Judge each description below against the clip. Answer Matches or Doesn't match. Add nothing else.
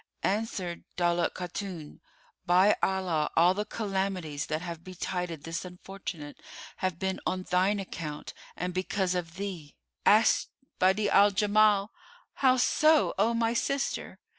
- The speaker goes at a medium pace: Doesn't match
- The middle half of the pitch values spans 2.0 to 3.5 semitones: Matches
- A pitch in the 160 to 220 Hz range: Matches